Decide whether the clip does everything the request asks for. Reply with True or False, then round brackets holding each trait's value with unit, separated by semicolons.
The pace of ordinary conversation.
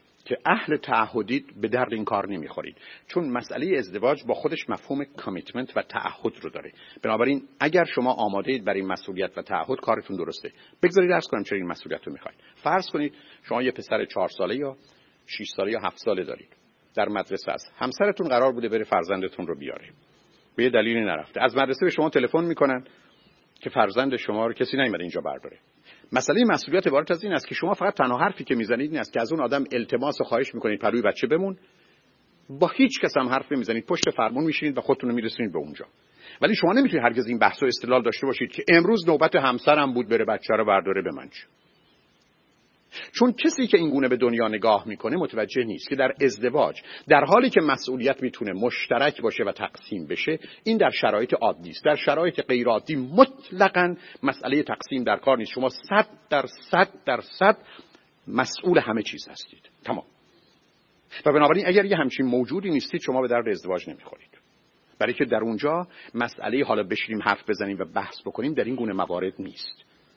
False (190 wpm)